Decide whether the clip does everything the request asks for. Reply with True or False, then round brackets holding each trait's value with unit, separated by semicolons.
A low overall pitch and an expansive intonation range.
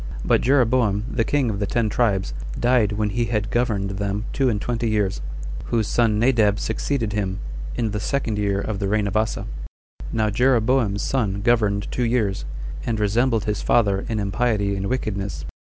False (110 Hz; 2.9 semitones)